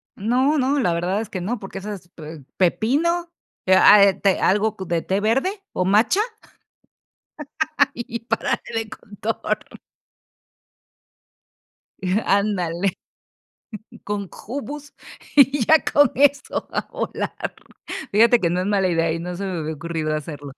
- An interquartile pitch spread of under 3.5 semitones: No, wide, 5.4 semitones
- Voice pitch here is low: No, high, 200 Hz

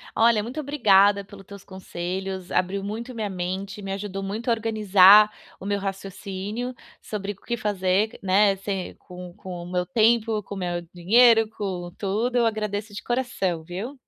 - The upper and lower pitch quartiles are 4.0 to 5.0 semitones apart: No, average, 2.7 semitones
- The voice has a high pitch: Yes, high, 200 Hz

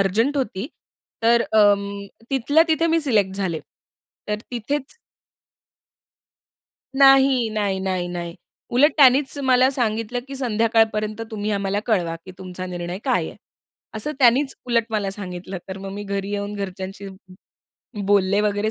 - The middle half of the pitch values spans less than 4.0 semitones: No, average, 4.3 semitones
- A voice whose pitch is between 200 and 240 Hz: Yes, high, 210 Hz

